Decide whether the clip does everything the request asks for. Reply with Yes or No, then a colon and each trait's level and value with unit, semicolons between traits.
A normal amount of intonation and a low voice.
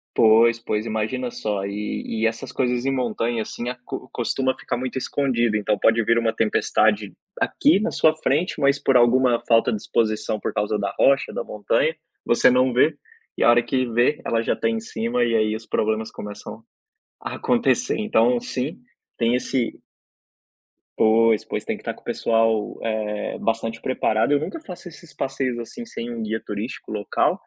Yes: average, 3.0 semitones; low, 115 Hz